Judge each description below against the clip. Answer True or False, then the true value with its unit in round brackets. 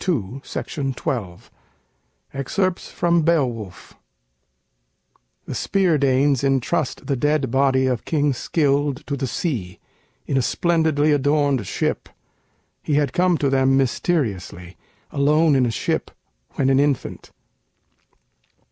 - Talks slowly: True (120 wpm)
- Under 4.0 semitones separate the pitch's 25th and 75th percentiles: True (2.7 semitones)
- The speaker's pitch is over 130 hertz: True (140 Hz)